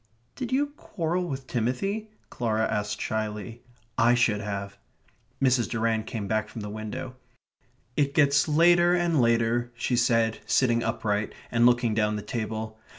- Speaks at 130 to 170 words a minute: Yes, average, 150 wpm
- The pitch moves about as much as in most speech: Yes, average, 4.2 semitones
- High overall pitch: No, low, 115 Hz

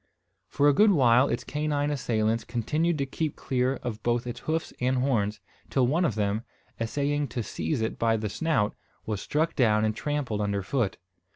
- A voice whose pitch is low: Yes, low, 125 Hz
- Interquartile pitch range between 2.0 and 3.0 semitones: No, average, 4.9 semitones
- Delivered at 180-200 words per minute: Yes, average, 185 wpm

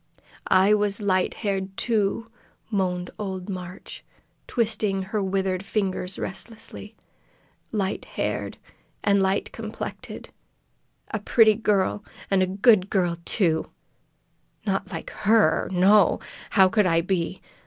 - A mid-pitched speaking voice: No, high, 195 Hz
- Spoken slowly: Yes, slow, 115 wpm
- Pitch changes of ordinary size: No, narrow, 2.2 semitones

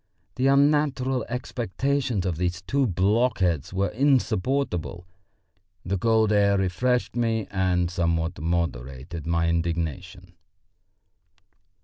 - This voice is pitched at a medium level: No, very low, 95 Hz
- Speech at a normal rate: No, slow, 100 wpm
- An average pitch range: No, wide, 6.3 semitones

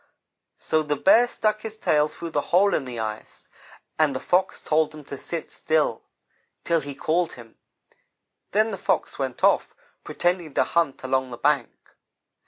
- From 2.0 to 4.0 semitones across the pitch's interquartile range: No, average, 4.5 semitones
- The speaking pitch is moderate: Yes, medium, 155 Hz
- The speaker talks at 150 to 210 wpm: Yes, average, 170 wpm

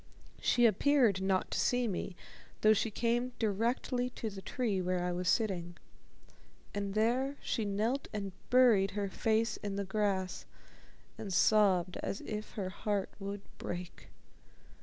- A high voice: Yes, high, 205 Hz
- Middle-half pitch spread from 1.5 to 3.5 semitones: Yes, average, 3.1 semitones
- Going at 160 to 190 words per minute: No, average, 145 wpm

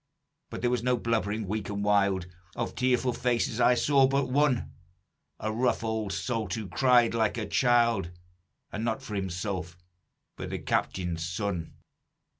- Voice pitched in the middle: No, low, 110 Hz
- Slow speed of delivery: No, average, 155 wpm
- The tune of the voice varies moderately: Yes, average, 3.5 semitones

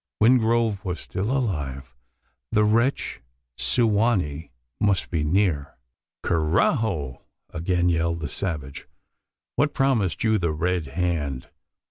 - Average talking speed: No, slow, 115 wpm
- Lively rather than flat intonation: Yes, wide, 6.1 semitones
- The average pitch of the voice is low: Yes, very low, 90 Hz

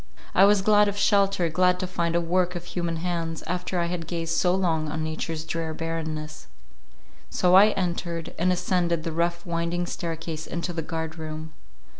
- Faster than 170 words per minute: Yes, average, 180 wpm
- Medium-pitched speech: Yes, medium, 170 Hz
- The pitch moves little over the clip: Yes, narrow, 1.8 semitones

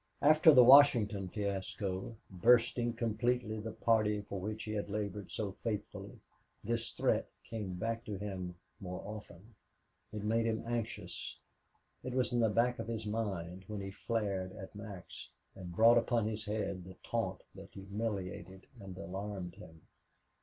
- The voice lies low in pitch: Yes, low, 105 Hz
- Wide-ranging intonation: No, average, 3.0 semitones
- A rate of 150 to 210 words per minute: Yes, average, 155 wpm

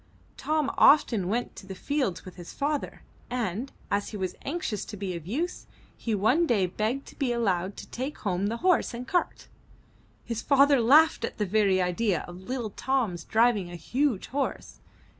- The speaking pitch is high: Yes, high, 230 Hz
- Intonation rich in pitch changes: Yes, wide, 6.2 semitones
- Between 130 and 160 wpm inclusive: No, average, 180 wpm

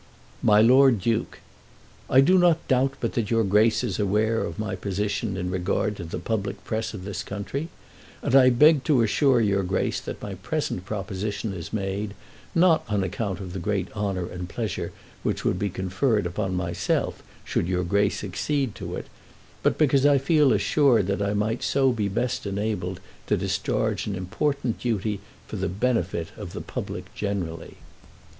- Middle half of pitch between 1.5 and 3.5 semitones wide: No, average, 4.4 semitones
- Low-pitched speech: Yes, low, 105 Hz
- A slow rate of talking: No, average, 175 wpm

